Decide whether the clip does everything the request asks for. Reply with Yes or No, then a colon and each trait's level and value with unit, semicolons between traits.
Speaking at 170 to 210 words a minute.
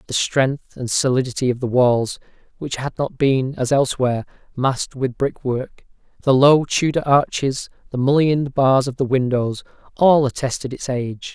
No: average, 155 wpm